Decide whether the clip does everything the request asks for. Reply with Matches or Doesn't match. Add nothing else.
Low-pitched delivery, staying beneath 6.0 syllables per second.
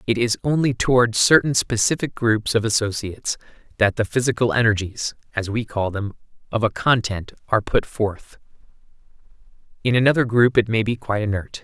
Matches